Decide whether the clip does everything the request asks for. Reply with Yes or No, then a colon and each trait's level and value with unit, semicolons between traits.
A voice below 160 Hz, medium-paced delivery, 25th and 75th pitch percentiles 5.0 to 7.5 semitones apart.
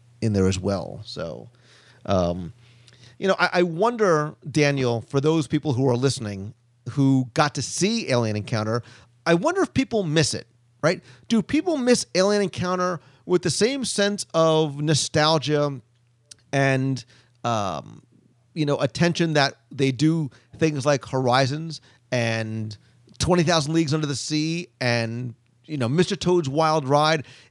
Yes: medium, 140 Hz; average, 145 wpm; wide, 5.4 semitones